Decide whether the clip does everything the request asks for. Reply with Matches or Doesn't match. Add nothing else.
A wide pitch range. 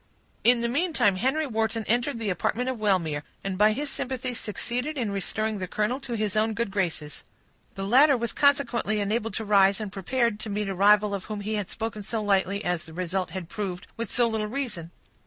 Doesn't match